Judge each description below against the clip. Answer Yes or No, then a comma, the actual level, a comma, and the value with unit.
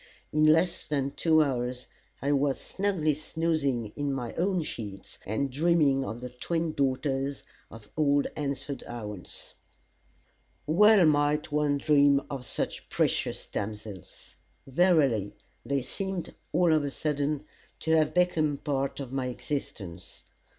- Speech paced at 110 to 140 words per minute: Yes, slow, 135 wpm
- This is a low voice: No, medium, 145 Hz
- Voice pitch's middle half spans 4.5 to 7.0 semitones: No, average, 3.3 semitones